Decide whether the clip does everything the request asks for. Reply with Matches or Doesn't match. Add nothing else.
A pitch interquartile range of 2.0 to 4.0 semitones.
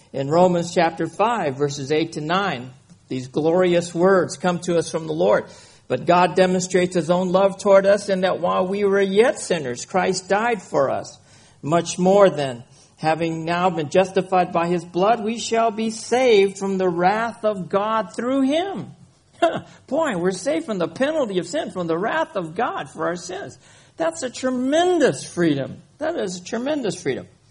Doesn't match